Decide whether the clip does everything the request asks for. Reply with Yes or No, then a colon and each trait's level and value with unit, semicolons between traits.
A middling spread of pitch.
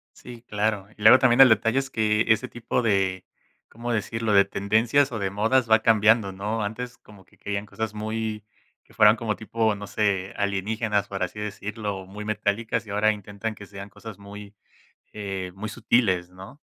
No: narrow, 2.0 semitones